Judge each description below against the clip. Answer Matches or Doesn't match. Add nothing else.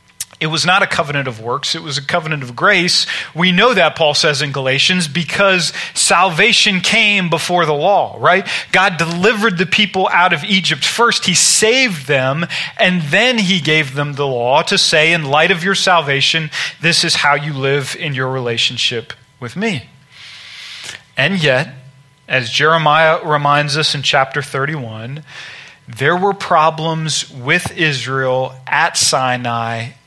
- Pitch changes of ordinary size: Matches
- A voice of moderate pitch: Matches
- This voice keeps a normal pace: Matches